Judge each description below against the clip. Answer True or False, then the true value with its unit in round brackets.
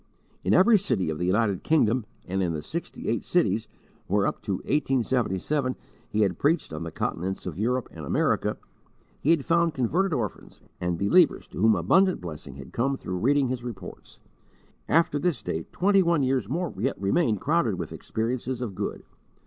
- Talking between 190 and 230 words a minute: False (180 wpm)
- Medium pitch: False (120 Hz)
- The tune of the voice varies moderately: False (7.6 semitones)